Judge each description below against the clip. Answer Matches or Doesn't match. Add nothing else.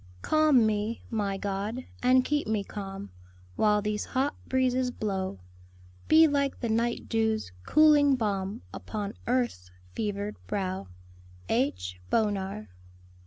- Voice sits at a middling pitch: Doesn't match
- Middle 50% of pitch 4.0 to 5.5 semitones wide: Matches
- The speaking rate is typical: Doesn't match